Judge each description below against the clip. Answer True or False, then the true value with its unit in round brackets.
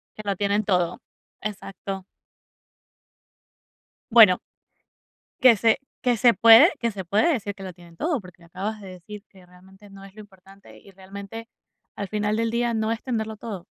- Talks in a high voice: True (205 Hz)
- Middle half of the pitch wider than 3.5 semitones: False (2.8 semitones)